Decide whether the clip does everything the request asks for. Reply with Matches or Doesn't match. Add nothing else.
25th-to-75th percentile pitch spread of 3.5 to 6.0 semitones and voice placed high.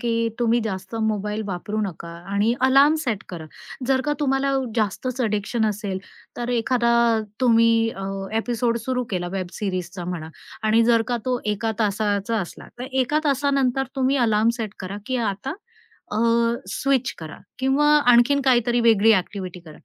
Matches